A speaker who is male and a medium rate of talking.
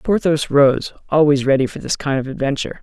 Yes: male; average, 190 wpm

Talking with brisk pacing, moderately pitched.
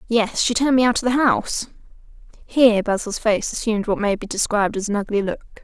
No: fast, 215 wpm; high, 220 Hz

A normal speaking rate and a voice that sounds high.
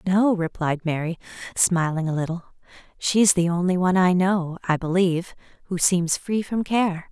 No: average, 160 wpm; medium, 180 Hz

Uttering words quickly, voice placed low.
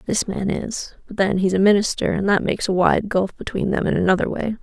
No: fast, 235 wpm; high, 195 Hz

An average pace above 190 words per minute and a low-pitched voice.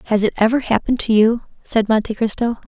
No: average, 200 wpm; high, 225 Hz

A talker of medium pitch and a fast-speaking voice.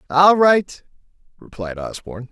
No: medium, 145 Hz; slow, 105 wpm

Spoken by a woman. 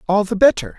No: male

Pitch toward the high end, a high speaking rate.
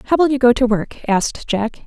Yes: high, 240 Hz; fast, 260 wpm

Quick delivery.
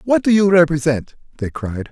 No: average, 190 wpm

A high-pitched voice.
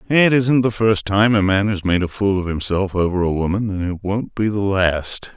No: low, 100 Hz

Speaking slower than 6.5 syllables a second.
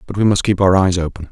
No: 6.8 syllables/s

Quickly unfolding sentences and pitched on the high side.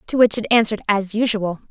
Yes: fast, 210 wpm; high, 215 Hz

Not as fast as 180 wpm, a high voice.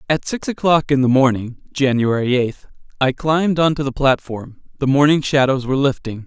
No: average, 170 wpm; low, 135 Hz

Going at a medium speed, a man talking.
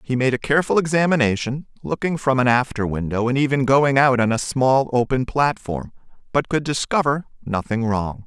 Yes: average, 175 wpm; male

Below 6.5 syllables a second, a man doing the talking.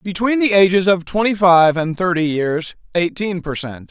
Yes: 4.5 syllables/s; male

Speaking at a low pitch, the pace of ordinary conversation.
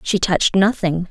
No: medium, 185 Hz; average, 165 wpm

